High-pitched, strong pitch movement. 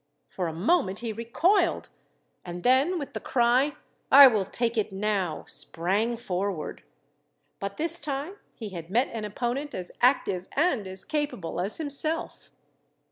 Yes: high, 230 Hz; wide, 6.8 semitones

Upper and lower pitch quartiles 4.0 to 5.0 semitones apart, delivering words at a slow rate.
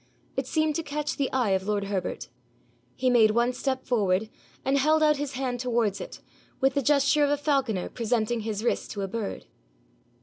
No: average, 4.6 semitones; average, 195 wpm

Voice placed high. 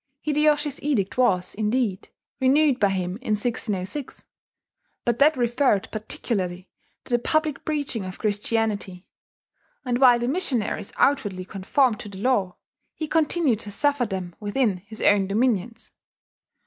Yes: high, 230 Hz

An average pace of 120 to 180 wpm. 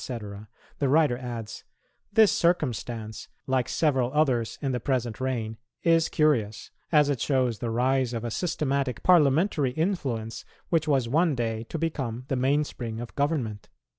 Yes: average, 150 wpm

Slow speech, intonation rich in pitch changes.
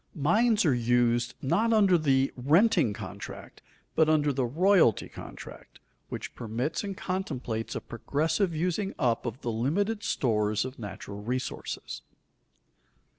Yes: slow, 125 wpm; wide, 7.6 semitones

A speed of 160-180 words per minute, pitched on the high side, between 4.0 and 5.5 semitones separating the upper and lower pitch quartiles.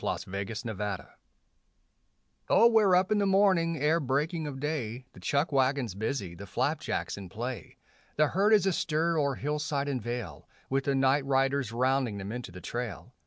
No: average, 170 wpm; low, 135 Hz; average, 5.2 semitones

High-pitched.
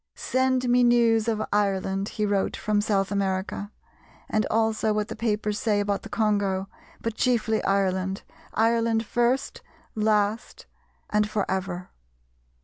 Yes: high, 210 Hz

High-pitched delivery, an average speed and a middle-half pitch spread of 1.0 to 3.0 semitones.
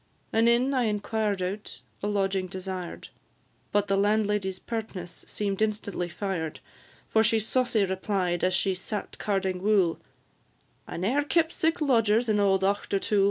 Yes: high, 205 Hz; average, 145 wpm; narrow, 2.6 semitones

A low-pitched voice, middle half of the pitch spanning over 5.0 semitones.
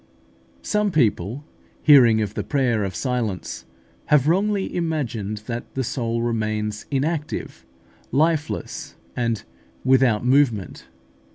Yes: low, 125 Hz; wide, 5.4 semitones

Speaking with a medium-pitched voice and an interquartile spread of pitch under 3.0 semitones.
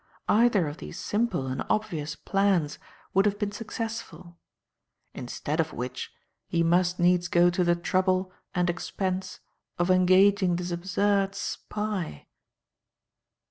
Yes: medium, 180 Hz; narrow, 2.5 semitones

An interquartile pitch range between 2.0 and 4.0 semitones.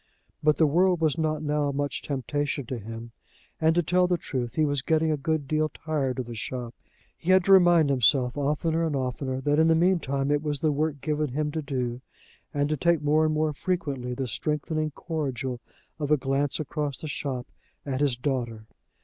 Yes: average, 2.9 semitones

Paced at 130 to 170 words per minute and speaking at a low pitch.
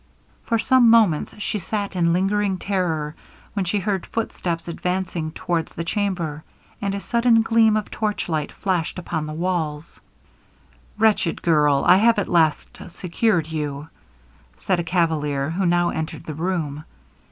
No: average, 145 wpm; medium, 175 Hz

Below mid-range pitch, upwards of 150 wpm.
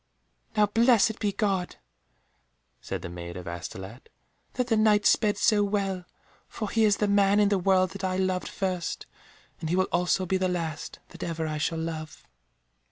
No: high, 190 Hz; average, 180 wpm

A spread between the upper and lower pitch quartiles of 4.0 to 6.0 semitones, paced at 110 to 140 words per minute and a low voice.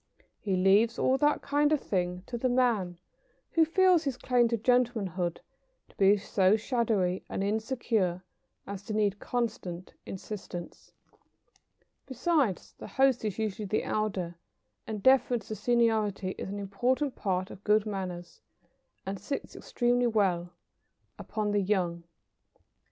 No: average, 4.4 semitones; slow, 135 wpm; high, 210 Hz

